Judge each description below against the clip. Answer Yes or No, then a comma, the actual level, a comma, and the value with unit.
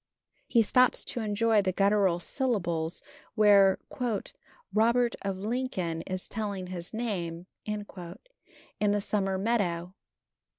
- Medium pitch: No, high, 200 Hz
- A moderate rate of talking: No, slow, 110 wpm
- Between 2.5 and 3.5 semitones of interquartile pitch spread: Yes, average, 3.1 semitones